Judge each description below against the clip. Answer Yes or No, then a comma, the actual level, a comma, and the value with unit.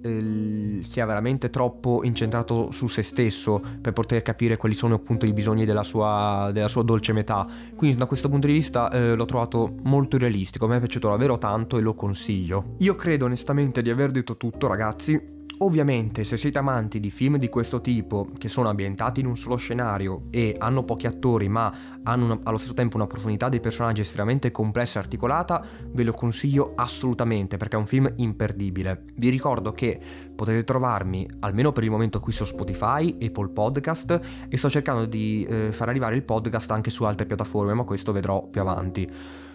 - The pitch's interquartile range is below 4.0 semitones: Yes, average, 3.0 semitones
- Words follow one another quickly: Yes, fast, 185 wpm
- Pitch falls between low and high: No, low, 115 Hz